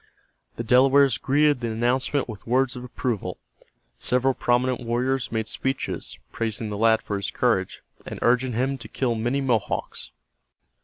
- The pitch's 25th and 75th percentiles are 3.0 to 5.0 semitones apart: No, narrow, 2.6 semitones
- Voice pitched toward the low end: Yes, low, 125 Hz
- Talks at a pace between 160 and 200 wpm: No, average, 150 wpm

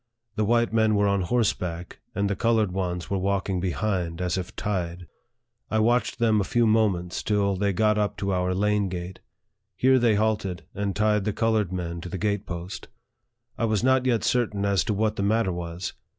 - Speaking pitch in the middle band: No, low, 100 Hz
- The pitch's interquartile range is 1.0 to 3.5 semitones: Yes, average, 3.1 semitones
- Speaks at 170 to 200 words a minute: Yes, average, 195 wpm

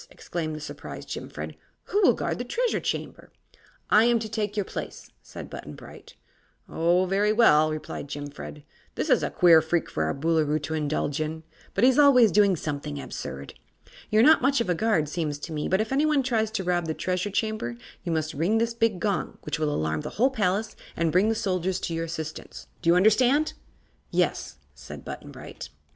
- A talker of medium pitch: Yes, medium, 180 Hz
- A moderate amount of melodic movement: No, wide, 6.0 semitones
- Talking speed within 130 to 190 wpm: No, average, 200 wpm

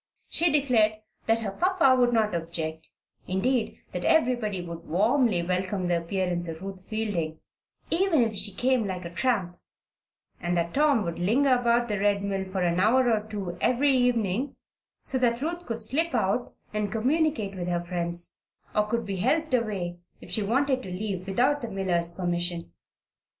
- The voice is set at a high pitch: Yes, high, 210 Hz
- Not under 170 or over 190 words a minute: Yes, average, 175 wpm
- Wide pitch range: Yes, wide, 5.7 semitones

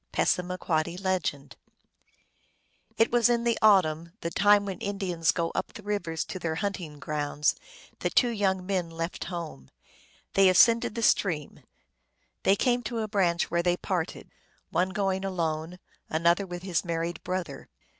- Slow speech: No, average, 150 wpm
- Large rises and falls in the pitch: No, average, 3.4 semitones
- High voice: No, medium, 180 Hz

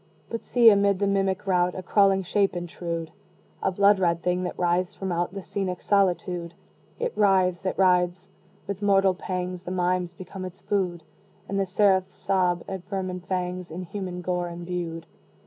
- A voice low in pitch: No, medium, 185 Hz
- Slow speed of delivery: No, average, 170 wpm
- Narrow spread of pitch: Yes, narrow, 1.6 semitones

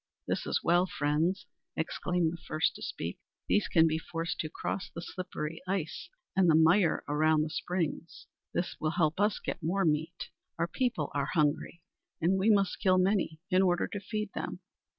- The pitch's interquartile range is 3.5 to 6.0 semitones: No, average, 2.9 semitones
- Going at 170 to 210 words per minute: Yes, average, 185 wpm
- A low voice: No, medium, 170 Hz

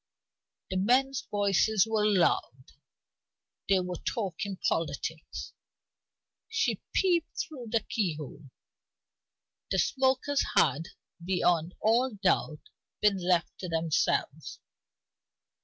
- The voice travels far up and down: Yes, wide, 5.7 semitones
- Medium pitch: No, high, 195 Hz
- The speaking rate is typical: No, slow, 90 wpm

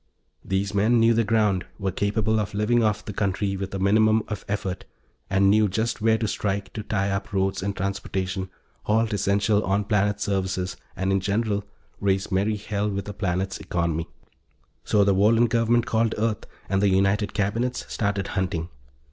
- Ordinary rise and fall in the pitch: No, narrow, 1.9 semitones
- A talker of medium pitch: No, low, 100 Hz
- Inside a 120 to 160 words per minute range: No, average, 175 wpm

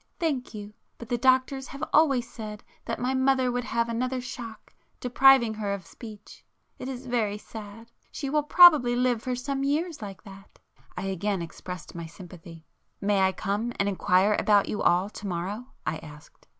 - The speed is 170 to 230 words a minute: Yes, average, 175 wpm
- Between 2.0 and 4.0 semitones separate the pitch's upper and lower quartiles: No, average, 4.5 semitones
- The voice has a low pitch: No, high, 230 Hz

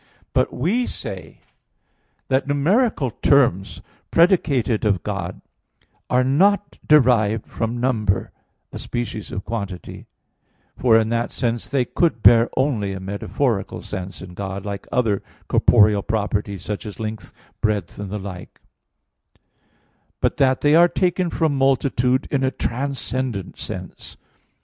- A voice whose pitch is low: Yes, low, 115 Hz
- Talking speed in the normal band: No, slow, 130 wpm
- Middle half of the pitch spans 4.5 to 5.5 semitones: Yes, average, 5.2 semitones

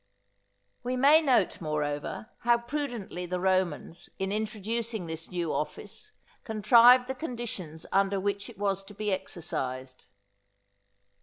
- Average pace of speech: No, slow, 125 wpm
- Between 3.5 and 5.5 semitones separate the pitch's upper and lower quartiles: Yes, average, 5.1 semitones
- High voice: Yes, high, 200 Hz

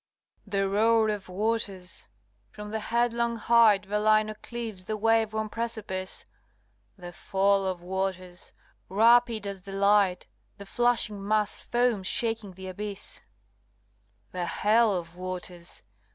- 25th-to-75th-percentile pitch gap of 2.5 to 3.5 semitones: Yes, average, 2.9 semitones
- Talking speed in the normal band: No, slow, 125 wpm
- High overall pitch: Yes, high, 205 Hz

